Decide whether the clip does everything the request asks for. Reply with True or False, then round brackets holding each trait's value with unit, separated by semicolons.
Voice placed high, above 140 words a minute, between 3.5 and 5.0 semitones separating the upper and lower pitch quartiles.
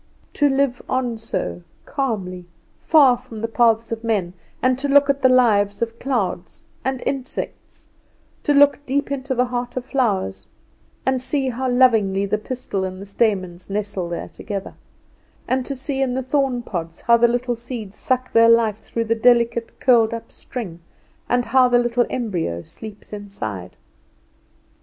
True (235 Hz; 165 wpm; 4.1 semitones)